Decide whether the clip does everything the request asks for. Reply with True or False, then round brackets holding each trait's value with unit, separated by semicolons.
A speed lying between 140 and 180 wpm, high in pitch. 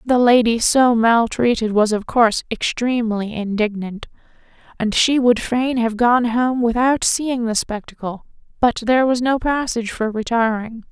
True (150 wpm; 235 Hz)